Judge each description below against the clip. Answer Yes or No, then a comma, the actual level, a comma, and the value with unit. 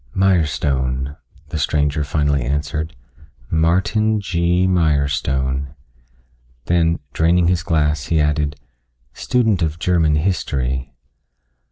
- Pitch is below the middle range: Yes, very low, 75 Hz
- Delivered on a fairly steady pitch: No, average, 3.4 semitones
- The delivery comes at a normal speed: No, slow, 90 wpm